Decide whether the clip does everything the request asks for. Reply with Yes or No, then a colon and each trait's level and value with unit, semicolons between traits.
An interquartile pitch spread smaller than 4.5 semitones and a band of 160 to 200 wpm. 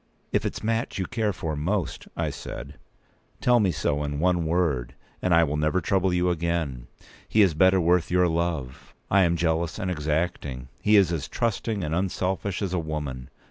Yes: average, 3.5 semitones; average, 190 wpm